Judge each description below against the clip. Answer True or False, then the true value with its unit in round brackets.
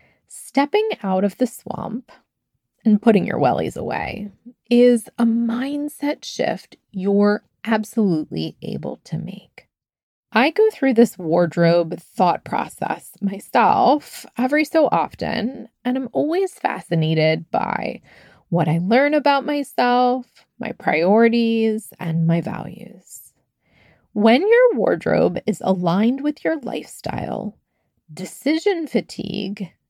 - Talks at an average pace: False (110 wpm)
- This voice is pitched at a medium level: False (225 Hz)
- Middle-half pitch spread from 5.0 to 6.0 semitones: True (5.4 semitones)